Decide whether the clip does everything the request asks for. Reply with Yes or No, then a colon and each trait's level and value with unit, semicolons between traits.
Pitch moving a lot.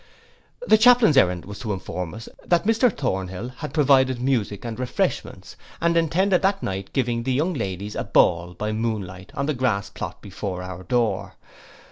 Yes: wide, 7.4 semitones